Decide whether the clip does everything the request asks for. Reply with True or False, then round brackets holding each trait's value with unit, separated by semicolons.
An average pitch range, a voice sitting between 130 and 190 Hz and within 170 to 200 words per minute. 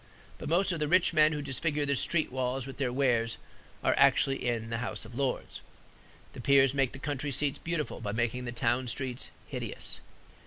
True (3.1 semitones; 135 Hz; 195 wpm)